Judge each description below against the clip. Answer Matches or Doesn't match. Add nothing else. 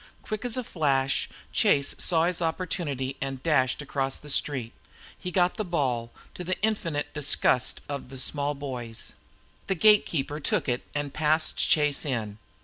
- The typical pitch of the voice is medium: Matches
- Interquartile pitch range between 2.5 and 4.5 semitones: Matches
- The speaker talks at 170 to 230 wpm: Doesn't match